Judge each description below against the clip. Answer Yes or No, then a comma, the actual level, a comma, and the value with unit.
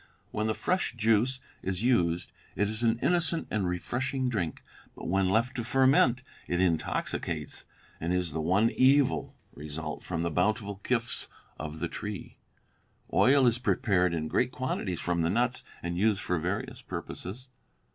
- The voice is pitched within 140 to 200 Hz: No, low, 105 Hz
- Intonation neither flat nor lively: No, wide, 6.0 semitones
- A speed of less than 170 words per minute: Yes, average, 155 wpm